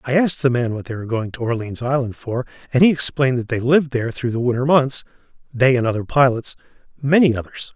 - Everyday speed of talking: No, fast, 215 wpm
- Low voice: Yes, low, 130 Hz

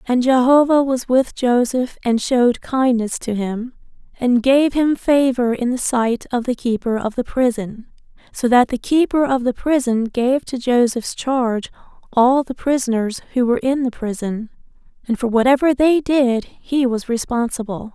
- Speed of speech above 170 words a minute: No, average, 165 wpm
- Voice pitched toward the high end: Yes, very high, 250 Hz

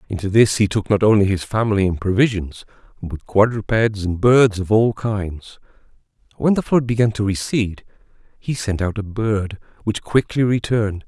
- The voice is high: No, low, 105 Hz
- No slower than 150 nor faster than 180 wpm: Yes, average, 170 wpm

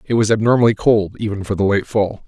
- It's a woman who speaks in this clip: No, male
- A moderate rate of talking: No, fast, 235 wpm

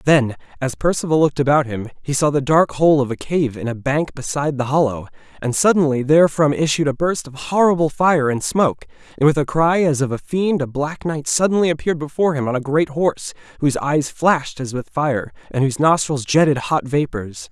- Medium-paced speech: No, fast, 210 wpm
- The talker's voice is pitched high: No, medium, 145 Hz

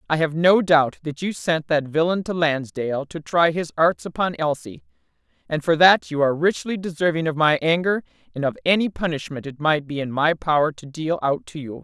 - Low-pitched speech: No, medium, 160 Hz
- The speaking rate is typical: No, fast, 215 wpm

